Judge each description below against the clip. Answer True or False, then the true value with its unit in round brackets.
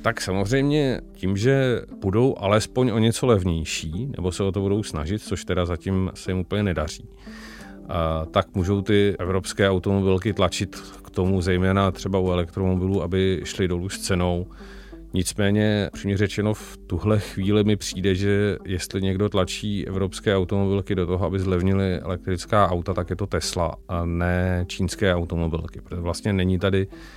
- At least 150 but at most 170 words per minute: True (155 wpm)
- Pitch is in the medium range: False (95 Hz)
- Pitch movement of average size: False (1.9 semitones)